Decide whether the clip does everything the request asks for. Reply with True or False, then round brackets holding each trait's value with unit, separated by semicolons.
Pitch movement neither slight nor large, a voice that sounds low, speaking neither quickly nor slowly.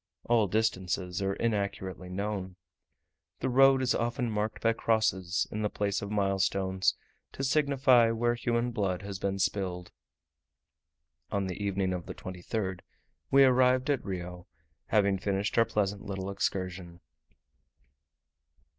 False (3.5 semitones; 100 Hz; 130 wpm)